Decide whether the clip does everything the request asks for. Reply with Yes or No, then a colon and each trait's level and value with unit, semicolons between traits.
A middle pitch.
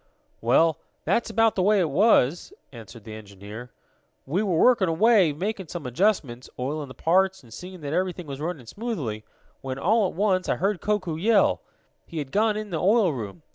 Yes: medium, 175 Hz